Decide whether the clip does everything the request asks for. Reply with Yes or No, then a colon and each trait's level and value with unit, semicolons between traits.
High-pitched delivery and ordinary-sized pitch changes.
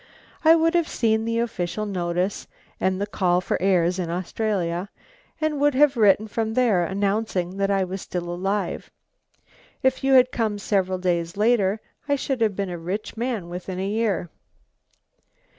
Yes: high, 200 Hz; average, 4.0 semitones